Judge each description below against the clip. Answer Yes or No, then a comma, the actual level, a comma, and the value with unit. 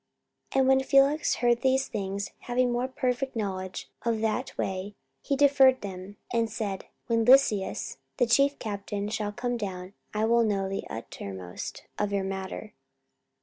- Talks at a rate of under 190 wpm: Yes, average, 155 wpm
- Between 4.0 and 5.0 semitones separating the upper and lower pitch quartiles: Yes, average, 4.4 semitones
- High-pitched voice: Yes, high, 220 Hz